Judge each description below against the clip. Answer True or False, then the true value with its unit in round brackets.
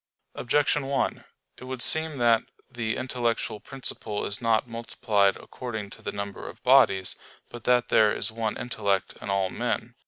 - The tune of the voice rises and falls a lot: False (3.2 semitones)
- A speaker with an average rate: True (160 wpm)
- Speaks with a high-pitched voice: False (115 Hz)